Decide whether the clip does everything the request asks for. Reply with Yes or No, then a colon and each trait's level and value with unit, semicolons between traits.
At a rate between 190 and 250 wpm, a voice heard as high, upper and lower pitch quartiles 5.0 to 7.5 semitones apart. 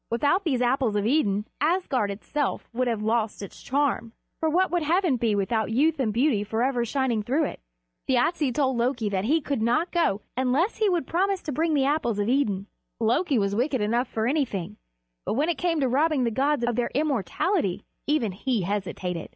Yes: average, 195 wpm; very high, 255 Hz; wide, 5.6 semitones